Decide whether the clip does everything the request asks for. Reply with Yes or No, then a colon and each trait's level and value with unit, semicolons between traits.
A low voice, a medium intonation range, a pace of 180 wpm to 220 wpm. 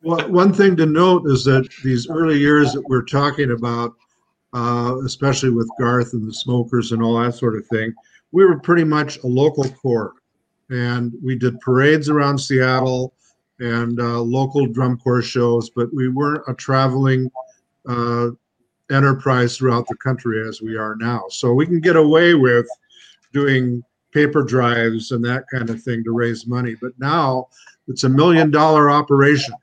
No: low, 130 Hz; average, 3.2 semitones; average, 170 wpm